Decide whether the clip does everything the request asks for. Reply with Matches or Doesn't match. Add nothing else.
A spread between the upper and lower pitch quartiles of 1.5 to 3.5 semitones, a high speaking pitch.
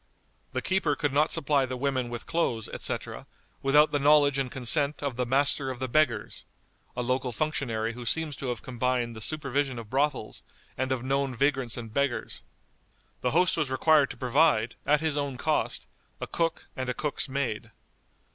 Doesn't match